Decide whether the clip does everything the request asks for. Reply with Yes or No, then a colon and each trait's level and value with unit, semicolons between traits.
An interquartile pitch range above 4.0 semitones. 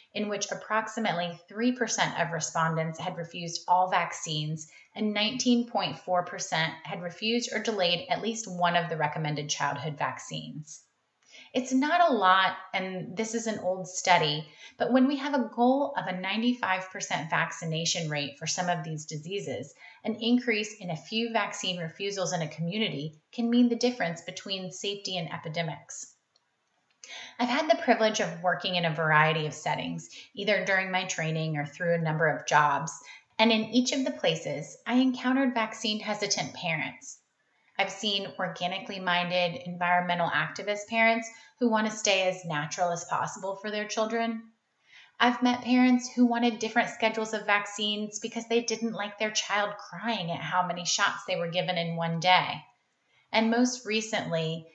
Yes: average, 4.7 semitones